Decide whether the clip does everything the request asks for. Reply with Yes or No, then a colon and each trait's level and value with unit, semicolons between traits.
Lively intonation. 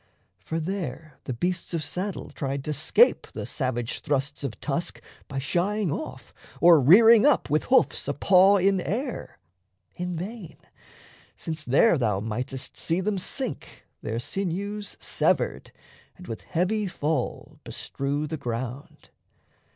Yes: wide, 6.2 semitones